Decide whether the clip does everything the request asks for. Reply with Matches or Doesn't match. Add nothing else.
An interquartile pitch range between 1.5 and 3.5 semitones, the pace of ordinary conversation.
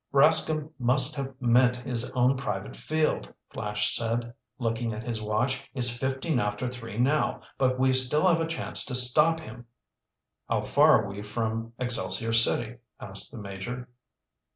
Matches